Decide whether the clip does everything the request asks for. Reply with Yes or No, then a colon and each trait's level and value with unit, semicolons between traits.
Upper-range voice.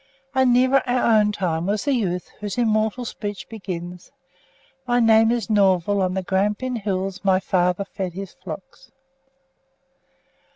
Yes: high, 205 Hz